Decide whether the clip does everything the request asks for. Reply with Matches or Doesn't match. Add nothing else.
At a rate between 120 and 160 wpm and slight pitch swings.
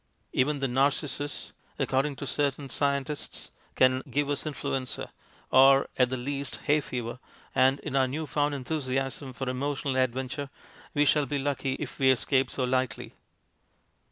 Matches